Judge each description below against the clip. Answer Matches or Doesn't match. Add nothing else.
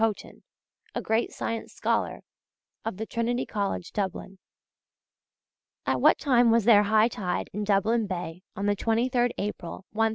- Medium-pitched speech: Doesn't match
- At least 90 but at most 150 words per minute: Matches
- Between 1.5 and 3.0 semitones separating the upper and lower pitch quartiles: Matches